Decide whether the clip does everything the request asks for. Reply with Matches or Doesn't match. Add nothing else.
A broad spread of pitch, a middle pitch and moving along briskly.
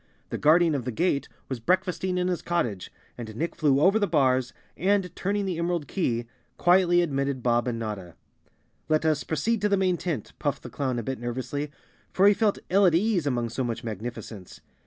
Matches